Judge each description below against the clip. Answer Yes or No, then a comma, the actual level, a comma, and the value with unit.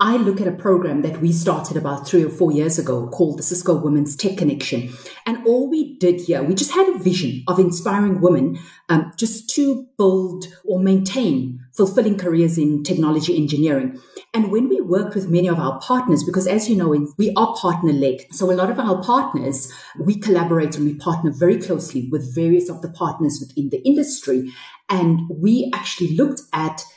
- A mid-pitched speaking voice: Yes, medium, 175 Hz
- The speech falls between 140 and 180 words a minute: No, average, 190 wpm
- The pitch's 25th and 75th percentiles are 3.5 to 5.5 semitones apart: Yes, average, 4.6 semitones